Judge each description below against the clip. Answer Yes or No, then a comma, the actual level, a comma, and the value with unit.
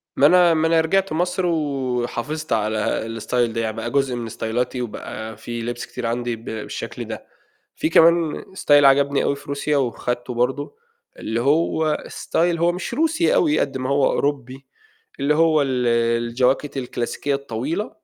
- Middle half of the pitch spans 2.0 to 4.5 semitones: No, average, 5.0 semitones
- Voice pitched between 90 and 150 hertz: Yes, medium, 140 Hz